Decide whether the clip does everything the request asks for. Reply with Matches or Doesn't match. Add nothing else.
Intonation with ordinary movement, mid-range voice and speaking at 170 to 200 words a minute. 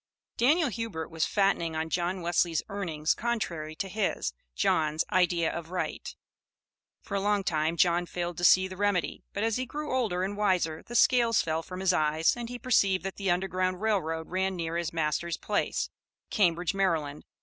Matches